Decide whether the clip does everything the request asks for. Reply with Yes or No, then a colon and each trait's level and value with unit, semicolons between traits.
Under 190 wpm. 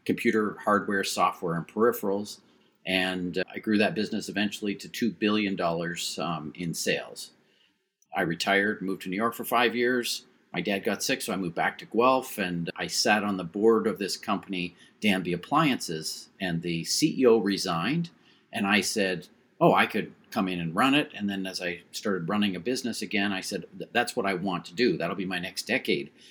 No: average, 195 wpm